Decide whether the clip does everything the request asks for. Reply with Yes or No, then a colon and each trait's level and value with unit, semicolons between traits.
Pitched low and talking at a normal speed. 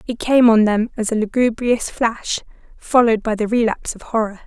No: high, 225 Hz; average, 190 wpm